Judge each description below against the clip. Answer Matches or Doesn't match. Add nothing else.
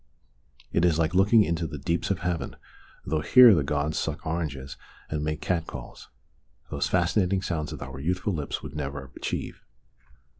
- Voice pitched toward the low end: Matches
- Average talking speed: Matches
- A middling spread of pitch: Matches